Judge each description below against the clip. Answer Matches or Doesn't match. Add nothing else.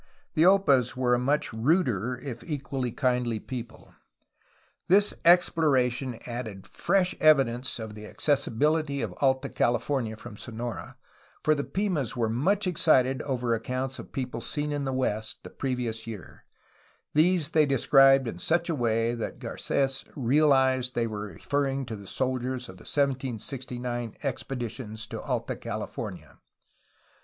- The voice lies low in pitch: Matches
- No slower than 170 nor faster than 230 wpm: Doesn't match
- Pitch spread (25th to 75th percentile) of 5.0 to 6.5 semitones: Doesn't match